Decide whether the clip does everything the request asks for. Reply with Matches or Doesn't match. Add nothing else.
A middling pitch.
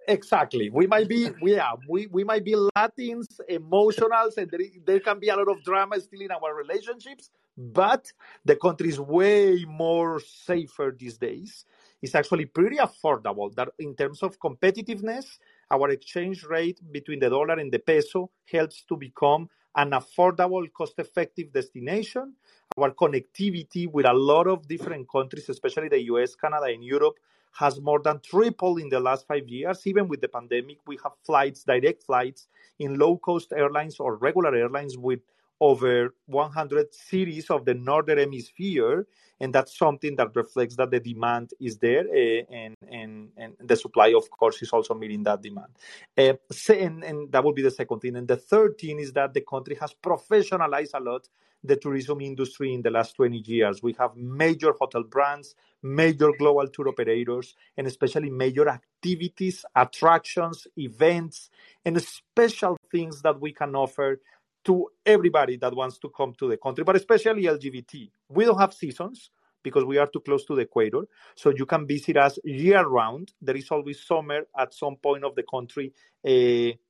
Matches